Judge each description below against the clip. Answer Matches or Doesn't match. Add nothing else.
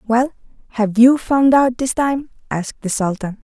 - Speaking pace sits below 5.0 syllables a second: Matches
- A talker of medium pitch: Doesn't match